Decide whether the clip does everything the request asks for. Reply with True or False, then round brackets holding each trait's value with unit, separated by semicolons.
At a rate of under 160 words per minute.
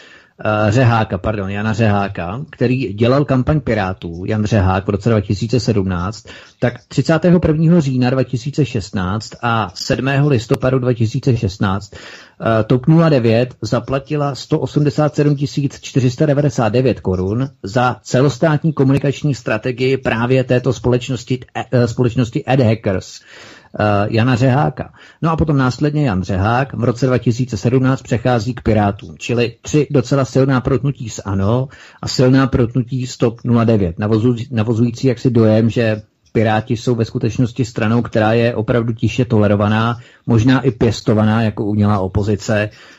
True (115 wpm)